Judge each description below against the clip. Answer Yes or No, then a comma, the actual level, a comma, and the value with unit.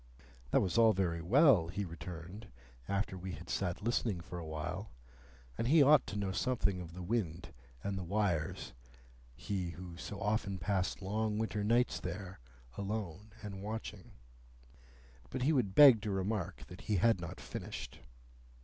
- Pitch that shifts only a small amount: No, average, 3.9 semitones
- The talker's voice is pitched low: Yes, very low, 95 Hz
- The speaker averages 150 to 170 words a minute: Yes, average, 160 wpm